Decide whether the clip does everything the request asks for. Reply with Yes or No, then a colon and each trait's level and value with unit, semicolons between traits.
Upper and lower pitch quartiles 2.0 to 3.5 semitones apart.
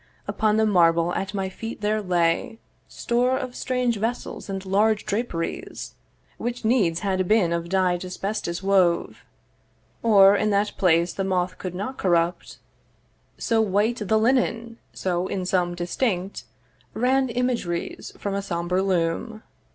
No: average, 3.9 semitones